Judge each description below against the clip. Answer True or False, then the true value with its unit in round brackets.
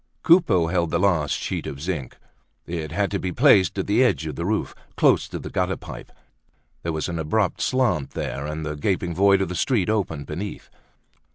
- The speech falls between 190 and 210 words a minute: True (200 wpm)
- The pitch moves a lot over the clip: False (4.3 semitones)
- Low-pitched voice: True (90 Hz)